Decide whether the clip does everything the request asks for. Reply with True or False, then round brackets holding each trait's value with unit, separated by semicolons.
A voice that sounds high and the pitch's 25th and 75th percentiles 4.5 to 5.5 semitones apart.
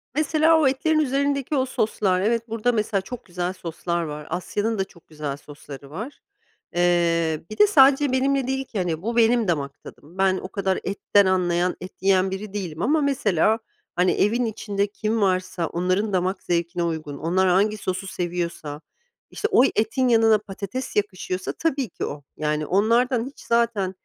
True (195 Hz; 5.1 semitones)